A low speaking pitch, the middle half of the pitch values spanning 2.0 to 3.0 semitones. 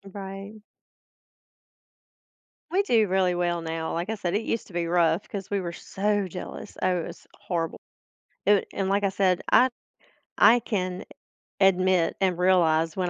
No: medium, 185 Hz; narrow, 2.4 semitones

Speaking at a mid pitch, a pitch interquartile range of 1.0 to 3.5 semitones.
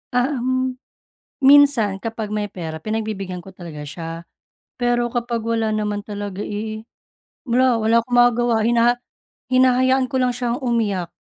No: high, 230 Hz; average, 3.1 semitones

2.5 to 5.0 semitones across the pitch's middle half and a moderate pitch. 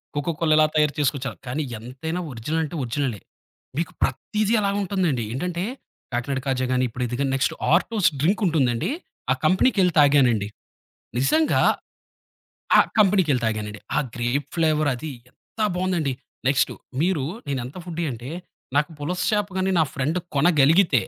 No: wide, 5.6 semitones; medium, 150 Hz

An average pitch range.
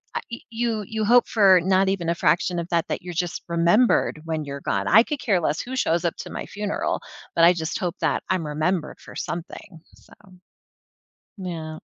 Yes: average, 3.9 semitones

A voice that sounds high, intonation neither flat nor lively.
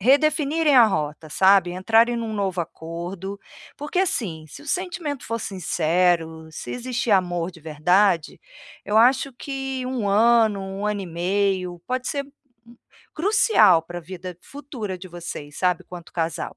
No: high, 195 Hz; wide, 6.3 semitones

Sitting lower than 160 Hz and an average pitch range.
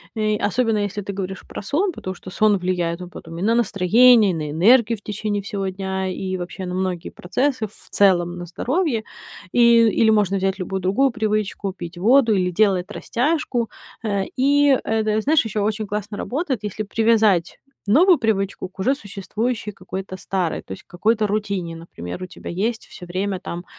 No: high, 205 Hz; average, 3.3 semitones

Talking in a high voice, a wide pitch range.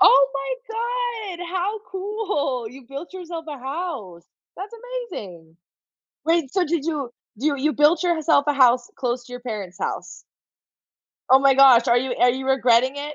Yes: very high, 280 Hz; wide, 6.0 semitones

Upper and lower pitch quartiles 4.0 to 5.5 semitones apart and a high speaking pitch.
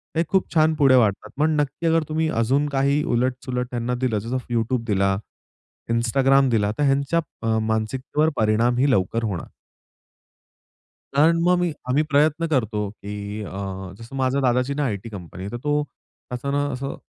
No: average, 4.5 semitones; low, 130 Hz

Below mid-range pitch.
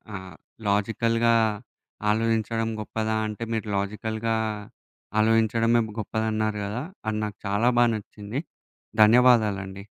Yes: low, 110 Hz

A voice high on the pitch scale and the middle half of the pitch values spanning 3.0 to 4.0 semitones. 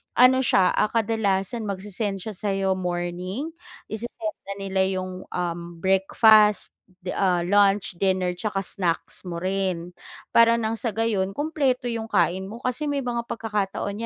Yes: high, 200 Hz; average, 3.4 semitones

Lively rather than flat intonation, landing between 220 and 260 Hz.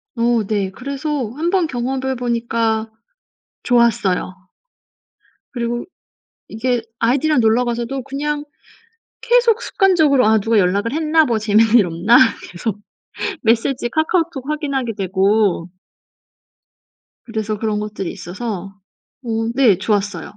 No: average, 4.3 semitones; high, 235 Hz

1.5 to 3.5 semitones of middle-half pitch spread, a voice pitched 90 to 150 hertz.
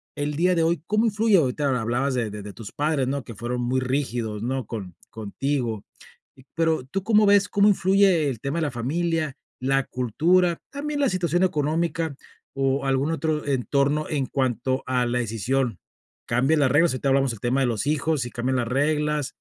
No: average, 4.6 semitones; medium, 140 Hz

